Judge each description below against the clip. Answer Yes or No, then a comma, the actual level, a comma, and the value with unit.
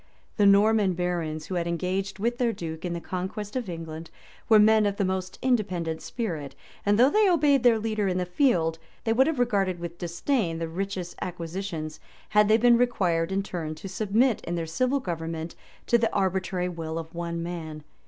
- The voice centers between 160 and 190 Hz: Yes, medium, 185 Hz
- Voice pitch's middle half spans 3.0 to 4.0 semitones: No, average, 4.6 semitones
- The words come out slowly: No, average, 195 wpm